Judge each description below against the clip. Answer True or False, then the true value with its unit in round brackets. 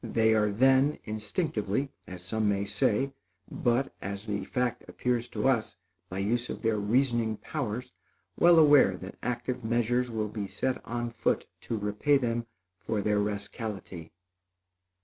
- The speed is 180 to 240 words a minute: False (150 wpm)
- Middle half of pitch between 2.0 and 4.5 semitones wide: True (3.3 semitones)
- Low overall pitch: True (115 Hz)